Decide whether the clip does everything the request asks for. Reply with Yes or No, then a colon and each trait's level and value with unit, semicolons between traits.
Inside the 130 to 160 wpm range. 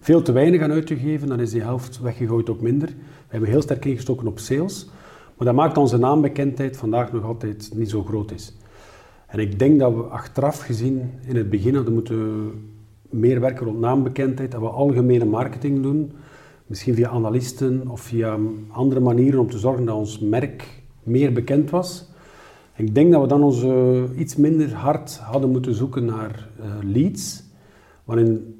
No: average, 180 wpm